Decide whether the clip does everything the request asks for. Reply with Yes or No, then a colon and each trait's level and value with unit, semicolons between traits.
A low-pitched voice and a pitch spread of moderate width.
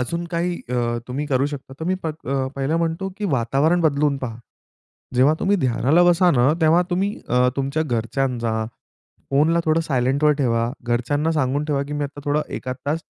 No: medium, 145 Hz; average, 4.2 semitones